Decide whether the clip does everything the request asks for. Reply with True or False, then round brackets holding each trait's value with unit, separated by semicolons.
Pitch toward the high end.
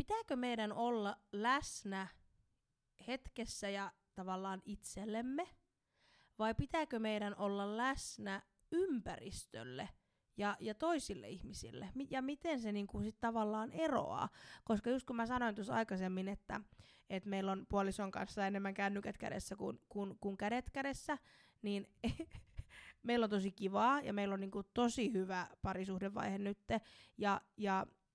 True (205 Hz)